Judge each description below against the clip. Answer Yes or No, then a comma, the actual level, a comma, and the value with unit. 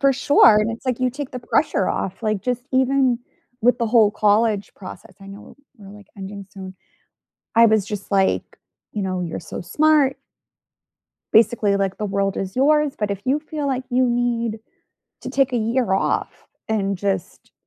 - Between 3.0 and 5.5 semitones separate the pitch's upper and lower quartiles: Yes, average, 4.4 semitones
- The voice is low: No, high, 220 Hz